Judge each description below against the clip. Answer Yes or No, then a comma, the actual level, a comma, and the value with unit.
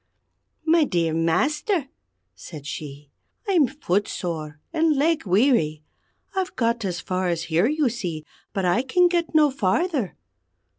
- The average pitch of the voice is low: No, high, 225 Hz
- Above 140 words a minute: No, slow, 135 wpm